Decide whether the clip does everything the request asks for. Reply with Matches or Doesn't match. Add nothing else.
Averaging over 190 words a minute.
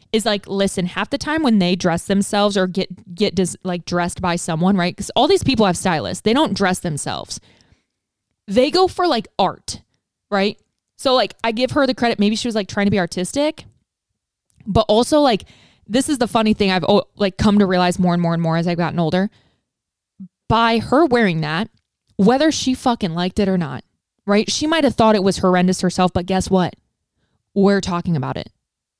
Matches